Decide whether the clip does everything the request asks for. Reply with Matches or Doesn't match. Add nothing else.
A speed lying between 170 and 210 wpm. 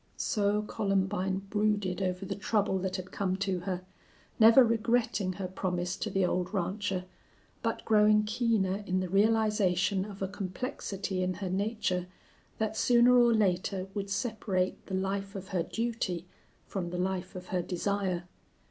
Doesn't match